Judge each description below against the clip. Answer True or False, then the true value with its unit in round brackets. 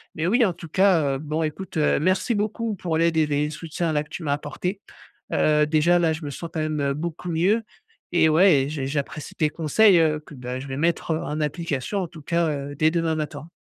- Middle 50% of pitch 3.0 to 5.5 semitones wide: False (2.5 semitones)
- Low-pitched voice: False (160 Hz)